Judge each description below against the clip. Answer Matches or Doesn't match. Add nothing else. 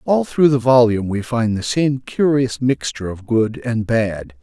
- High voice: Doesn't match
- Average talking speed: Matches